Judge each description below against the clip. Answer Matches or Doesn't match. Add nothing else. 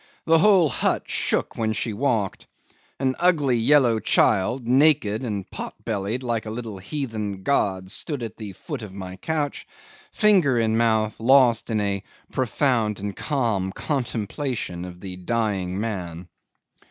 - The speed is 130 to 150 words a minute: Matches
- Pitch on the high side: Doesn't match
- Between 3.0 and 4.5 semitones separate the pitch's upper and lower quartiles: Doesn't match